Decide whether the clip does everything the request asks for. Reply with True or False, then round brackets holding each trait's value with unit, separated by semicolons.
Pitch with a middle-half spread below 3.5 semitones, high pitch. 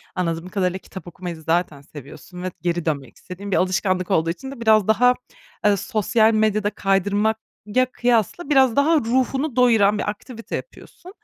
False (4.4 semitones; 205 Hz)